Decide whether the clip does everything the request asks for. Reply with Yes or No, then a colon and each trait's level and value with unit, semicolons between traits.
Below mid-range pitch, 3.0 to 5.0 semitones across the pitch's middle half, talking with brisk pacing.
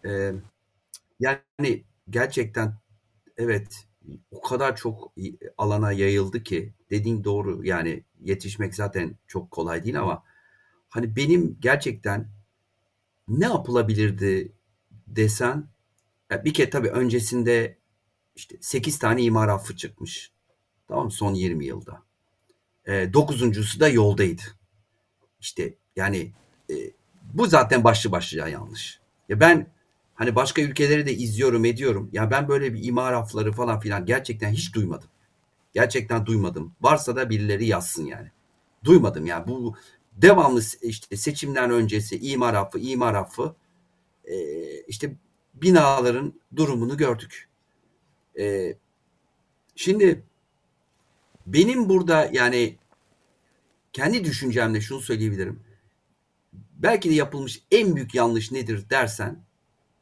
No: low, 115 Hz; average, 4.1 semitones; average, 115 wpm